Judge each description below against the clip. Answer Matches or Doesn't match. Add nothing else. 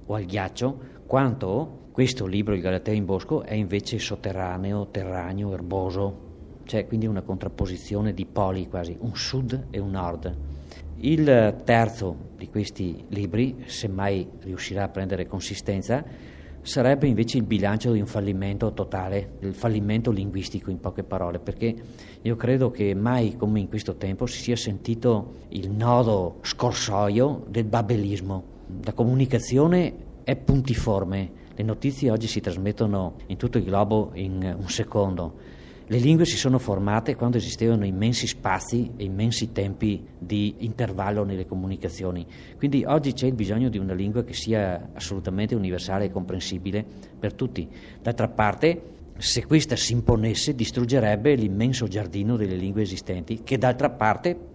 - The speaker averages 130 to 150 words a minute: Matches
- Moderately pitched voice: Doesn't match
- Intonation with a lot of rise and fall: Doesn't match